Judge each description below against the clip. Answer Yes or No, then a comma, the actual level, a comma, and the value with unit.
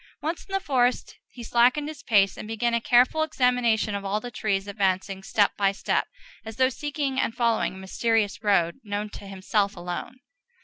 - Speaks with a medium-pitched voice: No, high, 220 Hz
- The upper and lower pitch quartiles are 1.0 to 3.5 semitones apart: No, average, 4.0 semitones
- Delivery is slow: No, average, 185 wpm